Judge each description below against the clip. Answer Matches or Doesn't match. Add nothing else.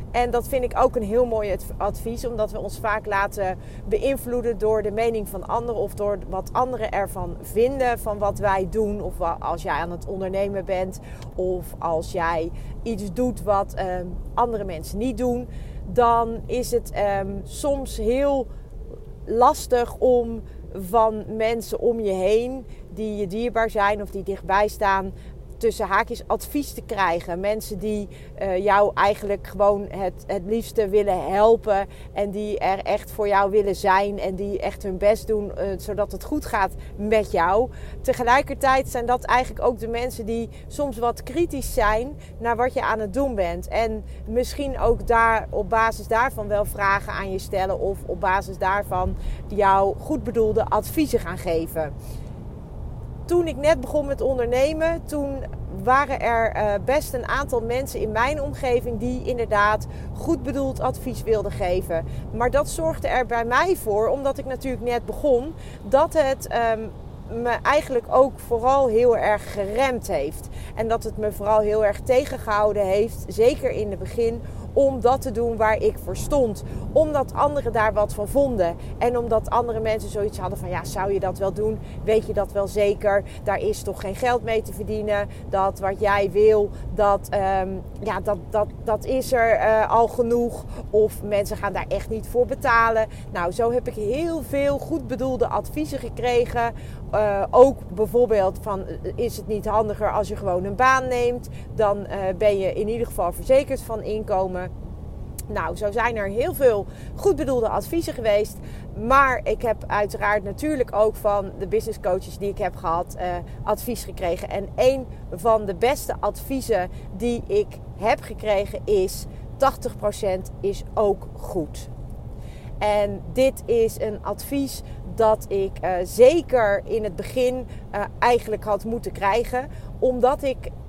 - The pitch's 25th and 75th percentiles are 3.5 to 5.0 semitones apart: Matches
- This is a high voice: Matches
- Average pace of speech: Matches